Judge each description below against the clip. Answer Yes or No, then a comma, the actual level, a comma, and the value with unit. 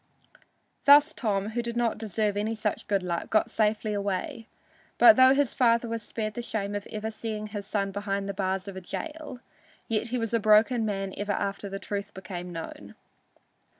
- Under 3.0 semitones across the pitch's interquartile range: Yes, narrow, 2.6 semitones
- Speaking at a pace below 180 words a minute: No, average, 190 wpm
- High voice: Yes, high, 215 Hz